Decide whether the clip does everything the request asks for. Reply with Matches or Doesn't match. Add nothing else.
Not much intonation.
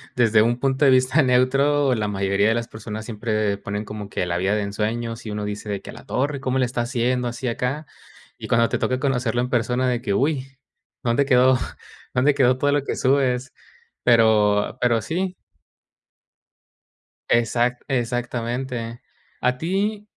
Doesn't match